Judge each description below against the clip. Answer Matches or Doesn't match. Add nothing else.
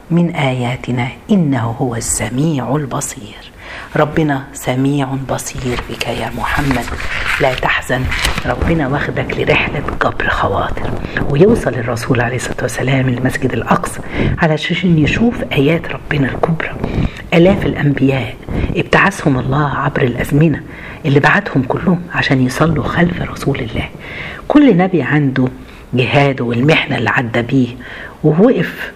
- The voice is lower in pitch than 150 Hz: Matches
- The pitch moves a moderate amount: Matches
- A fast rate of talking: Doesn't match